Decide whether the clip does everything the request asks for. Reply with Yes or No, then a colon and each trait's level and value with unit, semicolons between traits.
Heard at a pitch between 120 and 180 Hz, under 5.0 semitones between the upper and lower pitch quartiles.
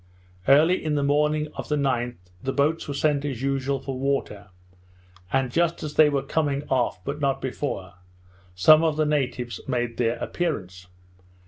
Yes: medium, 140 Hz; average, 3.0 semitones